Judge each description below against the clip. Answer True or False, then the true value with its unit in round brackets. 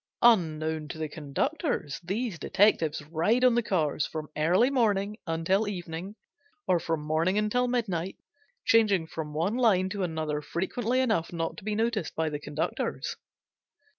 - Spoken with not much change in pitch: False (5.5 semitones)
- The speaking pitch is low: False (180 Hz)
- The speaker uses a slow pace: False (150 wpm)